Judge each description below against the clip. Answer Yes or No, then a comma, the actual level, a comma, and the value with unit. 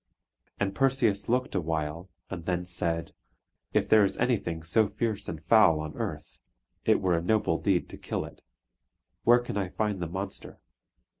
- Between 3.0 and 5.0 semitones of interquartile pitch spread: Yes, average, 4.6 semitones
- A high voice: No, very low, 95 Hz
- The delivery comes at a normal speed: Yes, average, 165 wpm